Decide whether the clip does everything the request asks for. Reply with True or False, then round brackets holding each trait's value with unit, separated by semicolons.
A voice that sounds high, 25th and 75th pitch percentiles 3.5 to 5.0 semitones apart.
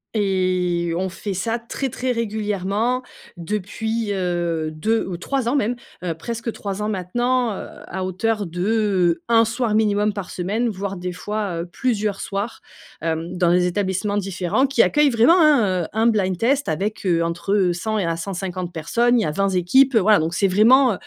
True (200 Hz; 4.1 semitones)